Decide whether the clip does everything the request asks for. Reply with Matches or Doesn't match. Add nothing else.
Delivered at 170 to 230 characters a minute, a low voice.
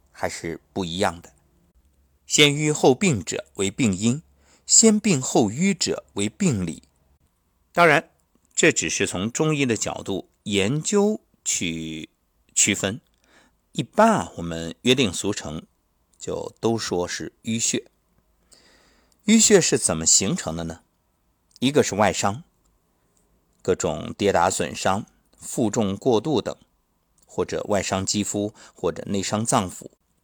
Matches